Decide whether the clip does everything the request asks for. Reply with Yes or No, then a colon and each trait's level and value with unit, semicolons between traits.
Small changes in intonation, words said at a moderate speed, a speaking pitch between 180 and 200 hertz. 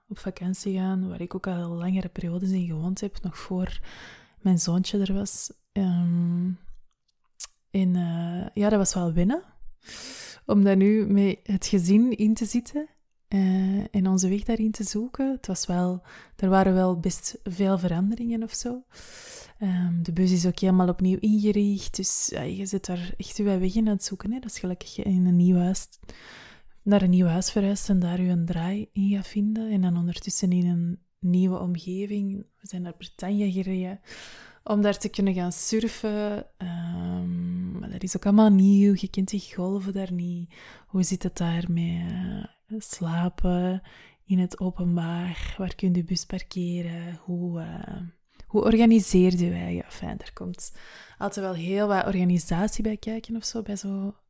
Yes: narrow, 2.2 semitones; average, 180 wpm; high, 190 Hz